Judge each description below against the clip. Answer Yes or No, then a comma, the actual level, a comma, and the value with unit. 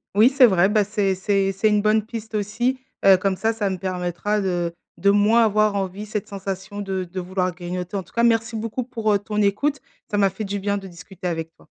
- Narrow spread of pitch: Yes, narrow, 2.2 semitones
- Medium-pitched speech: No, high, 200 Hz